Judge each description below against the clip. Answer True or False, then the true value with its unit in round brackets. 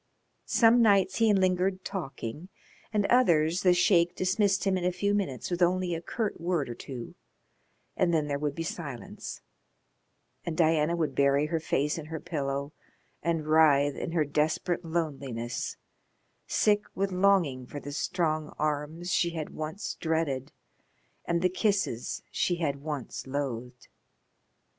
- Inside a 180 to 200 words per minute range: False (150 wpm)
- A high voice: False (165 Hz)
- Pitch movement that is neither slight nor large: True (4.1 semitones)